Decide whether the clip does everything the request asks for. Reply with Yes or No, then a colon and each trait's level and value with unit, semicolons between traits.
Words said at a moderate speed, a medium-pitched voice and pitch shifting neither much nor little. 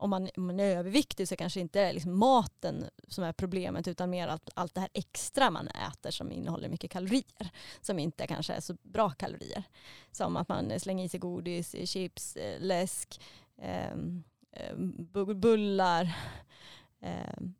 No: average, 165 wpm; medium, 180 Hz; narrow, 2.2 semitones